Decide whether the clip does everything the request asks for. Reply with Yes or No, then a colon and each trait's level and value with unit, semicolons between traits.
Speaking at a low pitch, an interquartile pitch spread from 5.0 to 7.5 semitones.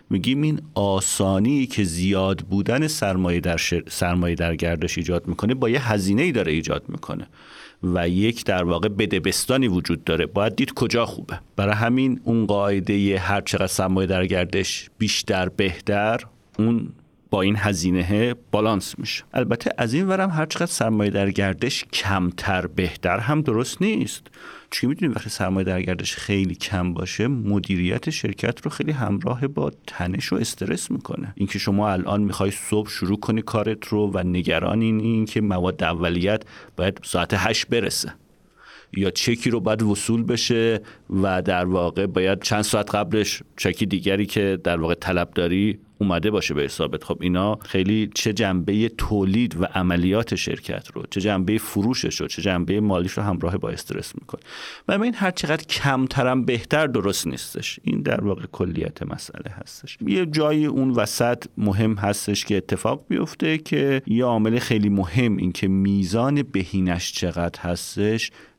No: low, 100 Hz; average, 3.3 semitones